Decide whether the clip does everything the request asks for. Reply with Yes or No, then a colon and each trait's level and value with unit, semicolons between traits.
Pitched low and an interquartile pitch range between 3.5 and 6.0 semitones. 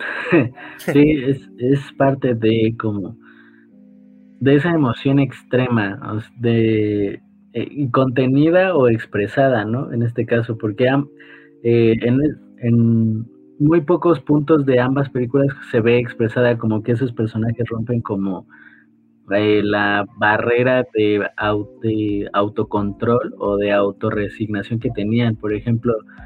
Yes: low, 115 Hz; average, 4.2 semitones